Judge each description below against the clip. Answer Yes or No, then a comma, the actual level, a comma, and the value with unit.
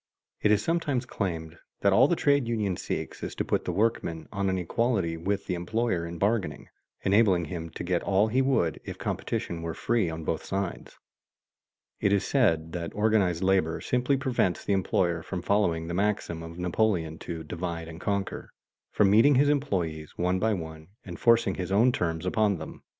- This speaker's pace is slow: No, average, 185 wpm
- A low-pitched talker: Yes, very low, 95 Hz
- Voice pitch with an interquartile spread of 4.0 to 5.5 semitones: Yes, average, 4.7 semitones